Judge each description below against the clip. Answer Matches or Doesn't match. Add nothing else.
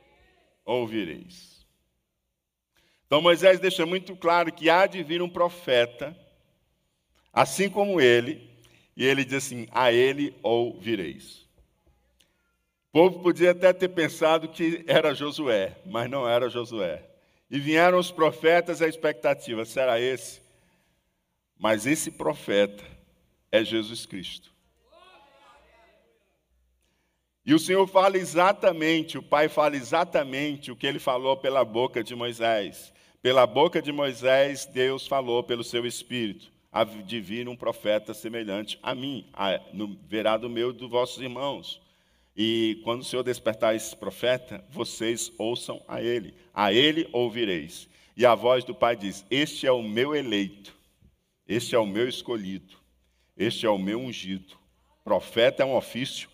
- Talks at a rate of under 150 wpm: Matches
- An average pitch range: Doesn't match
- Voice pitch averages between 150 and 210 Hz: Doesn't match